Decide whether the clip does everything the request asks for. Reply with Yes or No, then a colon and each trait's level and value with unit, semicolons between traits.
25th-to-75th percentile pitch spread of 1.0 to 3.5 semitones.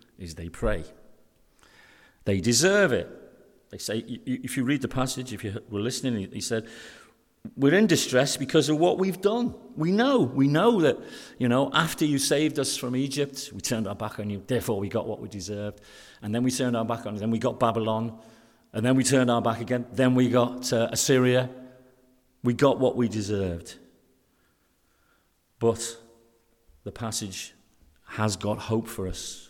Yes: average, 3.2 semitones